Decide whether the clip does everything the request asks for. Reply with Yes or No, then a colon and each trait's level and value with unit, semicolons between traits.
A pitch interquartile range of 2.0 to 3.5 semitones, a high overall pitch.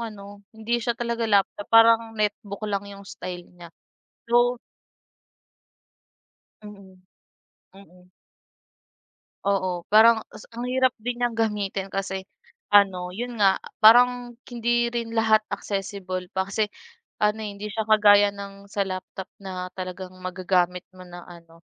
Yes: average, 3.1 semitones; high, 205 Hz